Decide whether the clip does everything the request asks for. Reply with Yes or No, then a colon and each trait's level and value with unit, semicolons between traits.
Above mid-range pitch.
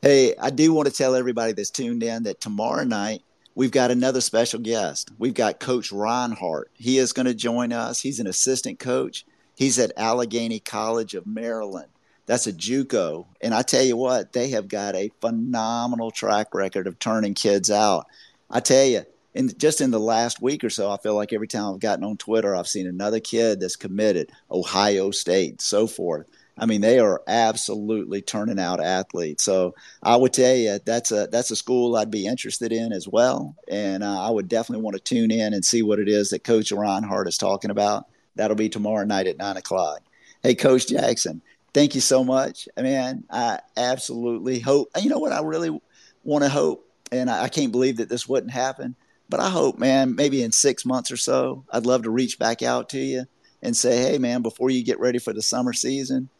No: low, 115 Hz